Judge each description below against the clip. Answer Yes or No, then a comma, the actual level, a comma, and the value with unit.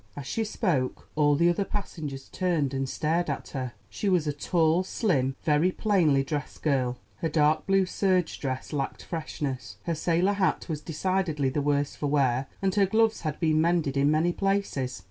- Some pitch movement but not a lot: Yes, average, 4.5 semitones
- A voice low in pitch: No, medium, 155 Hz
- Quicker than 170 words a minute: Yes, average, 185 wpm